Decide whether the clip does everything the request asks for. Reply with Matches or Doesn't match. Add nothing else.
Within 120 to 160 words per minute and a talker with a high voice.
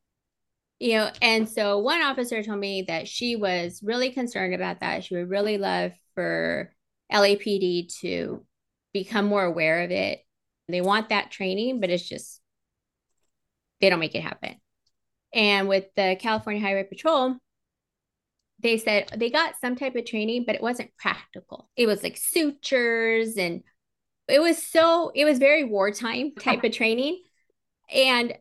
Matches